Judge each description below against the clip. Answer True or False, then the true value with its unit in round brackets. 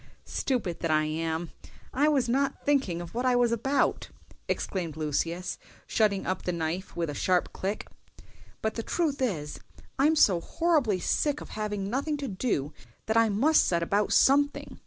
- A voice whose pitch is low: False (210 Hz)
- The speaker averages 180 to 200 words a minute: False (170 wpm)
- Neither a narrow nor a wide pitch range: False (7.9 semitones)